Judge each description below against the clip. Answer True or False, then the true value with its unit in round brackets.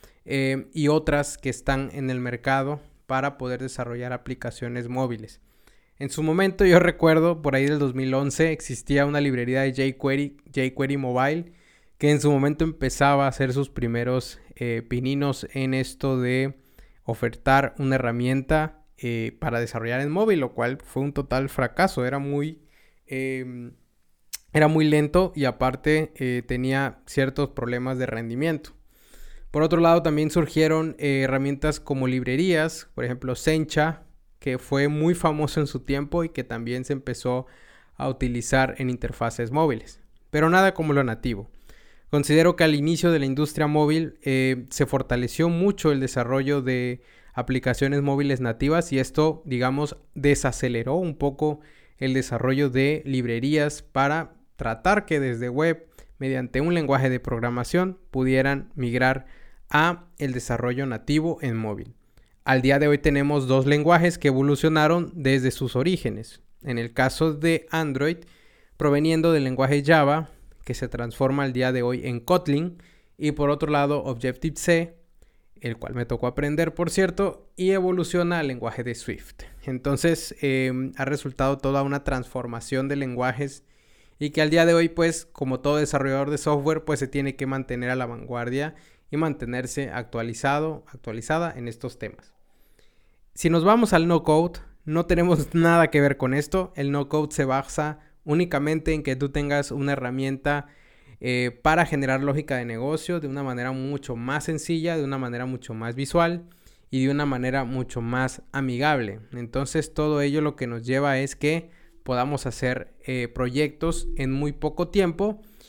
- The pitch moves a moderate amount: True (3.3 semitones)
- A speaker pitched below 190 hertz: True (140 Hz)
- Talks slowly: False (155 wpm)